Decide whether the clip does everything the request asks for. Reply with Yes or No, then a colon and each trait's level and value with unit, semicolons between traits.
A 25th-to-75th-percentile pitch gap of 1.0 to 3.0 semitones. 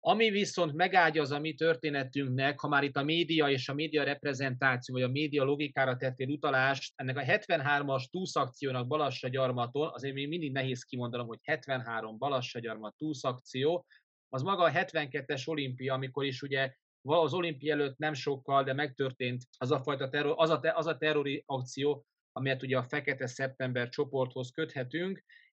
Yes: narrow, 2.6 semitones